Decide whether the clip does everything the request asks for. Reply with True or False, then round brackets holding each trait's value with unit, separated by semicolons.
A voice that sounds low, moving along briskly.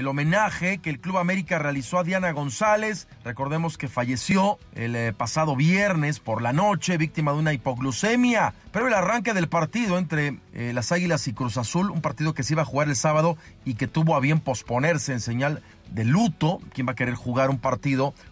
False (150 Hz; 200 wpm)